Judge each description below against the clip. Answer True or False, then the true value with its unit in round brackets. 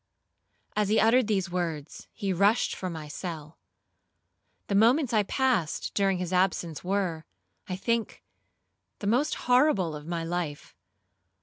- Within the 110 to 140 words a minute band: True (135 wpm)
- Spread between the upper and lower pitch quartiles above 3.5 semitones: True (4.7 semitones)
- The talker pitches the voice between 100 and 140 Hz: False (190 Hz)